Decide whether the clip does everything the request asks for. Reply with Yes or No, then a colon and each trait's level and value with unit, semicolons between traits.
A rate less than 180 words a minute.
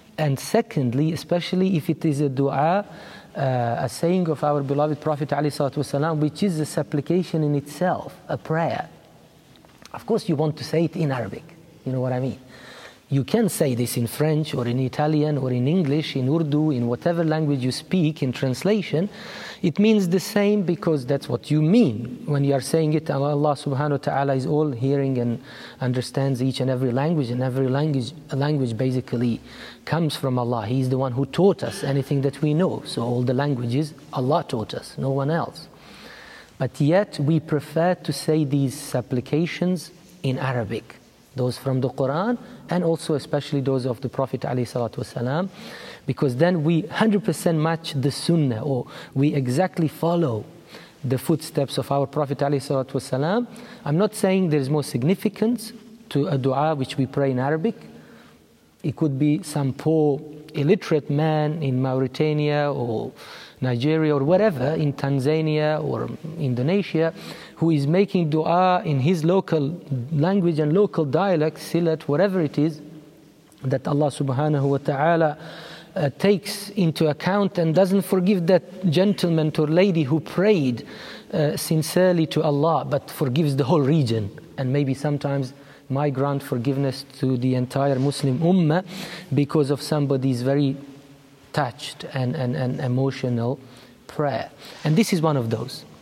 Yes: average, 155 wpm